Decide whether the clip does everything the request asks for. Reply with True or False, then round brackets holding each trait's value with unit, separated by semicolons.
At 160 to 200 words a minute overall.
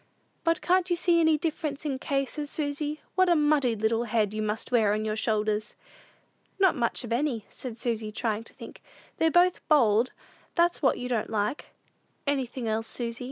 True (190 wpm)